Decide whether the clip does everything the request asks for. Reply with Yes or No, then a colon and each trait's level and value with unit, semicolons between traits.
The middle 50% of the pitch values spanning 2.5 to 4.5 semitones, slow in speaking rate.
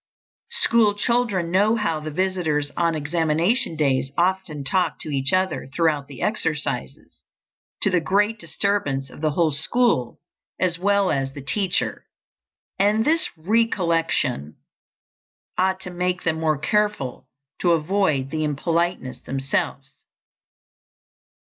No: average, 5.3 semitones; slow, 125 wpm